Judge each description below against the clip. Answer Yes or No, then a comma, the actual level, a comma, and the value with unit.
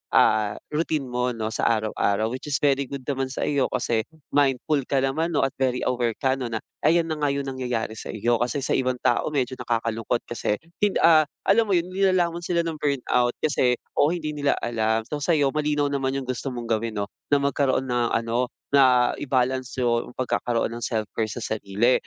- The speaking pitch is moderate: No, low, 130 Hz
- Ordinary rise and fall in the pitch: Yes, average, 3.6 semitones